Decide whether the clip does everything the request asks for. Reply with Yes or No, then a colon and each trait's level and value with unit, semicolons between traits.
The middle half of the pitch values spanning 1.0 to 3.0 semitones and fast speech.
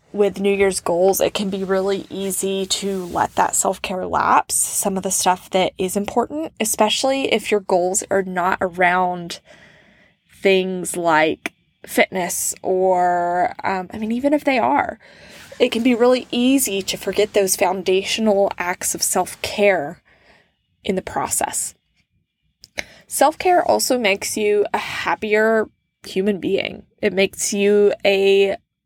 No: narrow, 2.4 semitones; average, 145 wpm